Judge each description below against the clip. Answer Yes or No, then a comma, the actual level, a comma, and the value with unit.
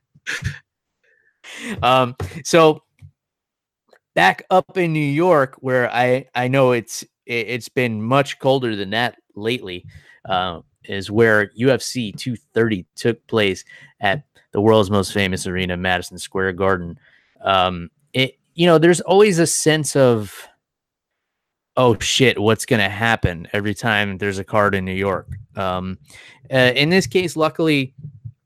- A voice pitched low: Yes, low, 120 Hz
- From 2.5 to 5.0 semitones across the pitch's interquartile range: No, wide, 5.4 semitones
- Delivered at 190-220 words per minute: No, slow, 135 wpm